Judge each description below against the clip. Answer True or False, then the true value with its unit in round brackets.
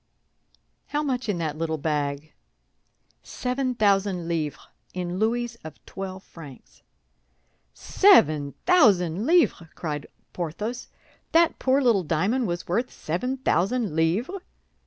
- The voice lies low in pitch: False (190 Hz)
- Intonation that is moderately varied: False (7.5 semitones)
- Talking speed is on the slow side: True (115 wpm)